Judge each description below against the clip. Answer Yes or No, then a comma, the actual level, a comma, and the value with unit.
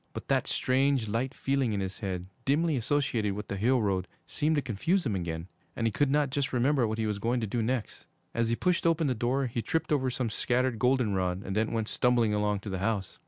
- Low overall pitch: Yes, low, 115 Hz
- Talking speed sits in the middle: No, fast, 235 wpm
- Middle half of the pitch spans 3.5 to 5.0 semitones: Yes, average, 4.4 semitones